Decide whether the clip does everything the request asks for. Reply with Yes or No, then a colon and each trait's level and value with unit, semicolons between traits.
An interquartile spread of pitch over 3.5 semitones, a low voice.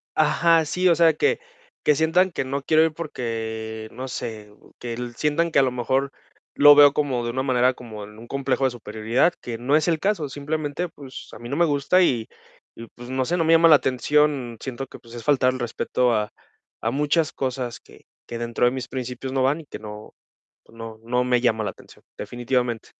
Yes: average, 4.0 semitones; low, 130 Hz